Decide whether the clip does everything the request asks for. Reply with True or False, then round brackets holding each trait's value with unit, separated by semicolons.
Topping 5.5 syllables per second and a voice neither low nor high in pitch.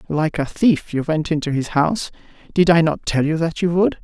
False (5.4 syllables/s; 155 Hz)